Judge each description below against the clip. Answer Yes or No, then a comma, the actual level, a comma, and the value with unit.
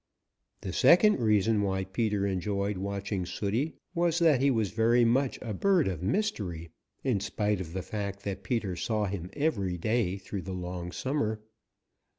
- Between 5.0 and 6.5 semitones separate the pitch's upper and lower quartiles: No, average, 4.2 semitones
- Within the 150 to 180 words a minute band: Yes, average, 165 wpm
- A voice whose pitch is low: Yes, low, 105 Hz